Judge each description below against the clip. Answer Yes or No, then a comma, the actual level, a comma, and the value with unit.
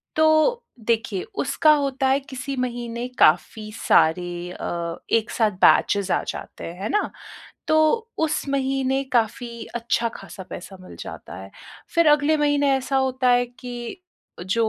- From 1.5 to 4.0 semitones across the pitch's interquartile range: No, average, 4.4 semitones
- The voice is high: Yes, high, 245 Hz